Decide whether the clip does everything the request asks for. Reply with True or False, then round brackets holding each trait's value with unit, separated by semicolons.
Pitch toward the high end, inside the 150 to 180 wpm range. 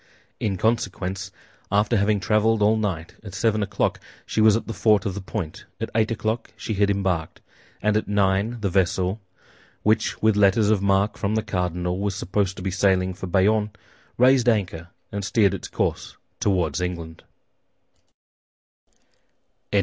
False (100 Hz; 155 wpm)